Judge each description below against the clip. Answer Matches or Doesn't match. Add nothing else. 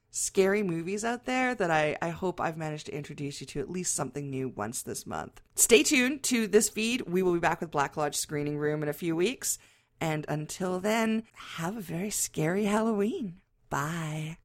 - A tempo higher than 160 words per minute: Matches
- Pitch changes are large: Matches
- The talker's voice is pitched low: Doesn't match